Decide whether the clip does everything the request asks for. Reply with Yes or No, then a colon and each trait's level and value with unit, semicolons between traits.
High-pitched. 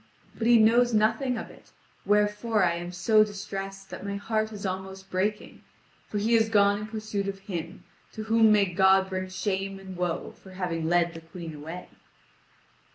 Yes: high, 195 Hz